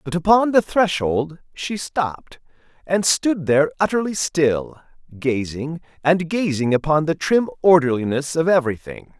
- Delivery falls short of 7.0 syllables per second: Yes, 4.5 syllables/s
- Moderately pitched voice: Yes, medium, 160 Hz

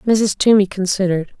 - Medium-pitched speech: No, high, 195 Hz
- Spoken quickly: No, slow, 130 wpm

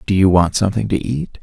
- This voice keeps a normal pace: No, fast, 255 wpm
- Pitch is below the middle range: Yes, very low, 95 Hz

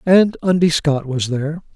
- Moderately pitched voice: Yes, medium, 160 Hz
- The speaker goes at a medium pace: Yes, average, 170 wpm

